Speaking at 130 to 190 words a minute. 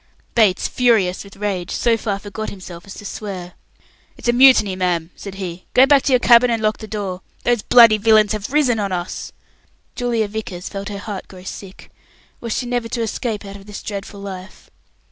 No: average, 200 wpm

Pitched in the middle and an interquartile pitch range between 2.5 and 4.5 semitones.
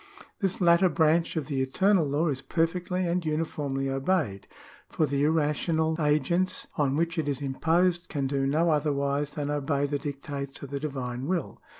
Yes: medium, 150 Hz; average, 3.2 semitones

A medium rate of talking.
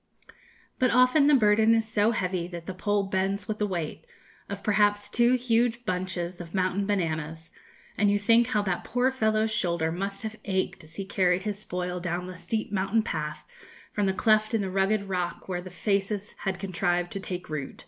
Yes: average, 195 wpm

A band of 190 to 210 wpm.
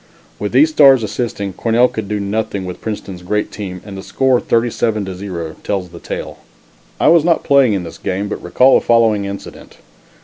Yes: average, 195 wpm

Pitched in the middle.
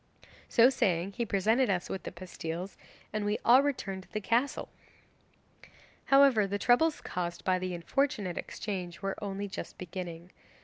No: high, 195 Hz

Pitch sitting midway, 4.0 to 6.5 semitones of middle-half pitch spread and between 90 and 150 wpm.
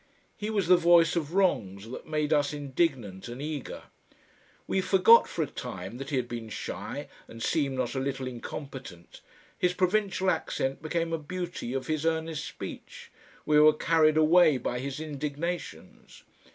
No: medium, 150 Hz; average, 4.5 semitones; average, 165 wpm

